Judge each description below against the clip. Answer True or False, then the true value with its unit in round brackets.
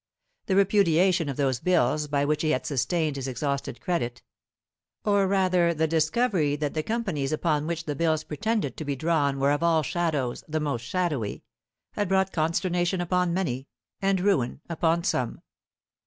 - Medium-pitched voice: True (160 Hz)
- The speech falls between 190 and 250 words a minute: False (165 wpm)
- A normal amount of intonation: True (4.1 semitones)